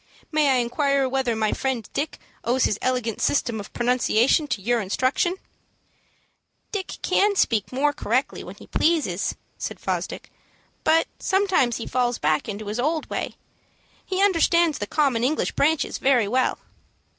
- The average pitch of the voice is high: Yes, very high, 255 Hz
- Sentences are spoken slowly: No, average, 150 wpm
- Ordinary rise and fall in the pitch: Yes, average, 4.9 semitones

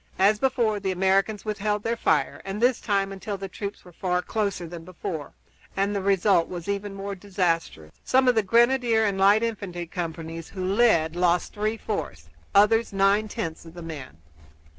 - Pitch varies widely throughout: No, average, 3.3 semitones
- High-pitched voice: Yes, high, 195 Hz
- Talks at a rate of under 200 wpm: Yes, average, 180 wpm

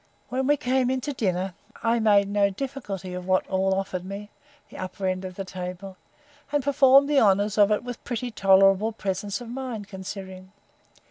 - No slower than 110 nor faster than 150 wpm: No, average, 185 wpm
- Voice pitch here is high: Yes, high, 200 Hz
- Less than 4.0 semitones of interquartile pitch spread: No, average, 4.5 semitones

